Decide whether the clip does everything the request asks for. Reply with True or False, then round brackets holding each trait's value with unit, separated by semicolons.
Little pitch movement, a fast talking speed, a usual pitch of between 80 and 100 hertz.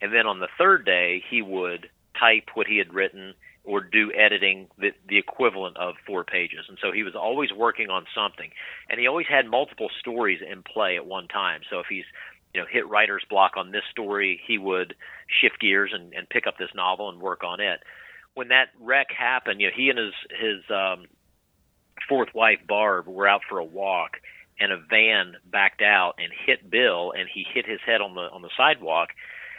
True (2.0 semitones; 210 wpm; 95 Hz)